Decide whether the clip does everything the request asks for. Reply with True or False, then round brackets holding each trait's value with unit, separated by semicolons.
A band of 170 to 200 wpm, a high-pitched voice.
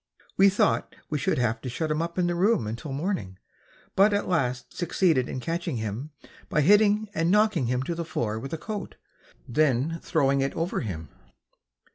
False (185 wpm; 155 Hz)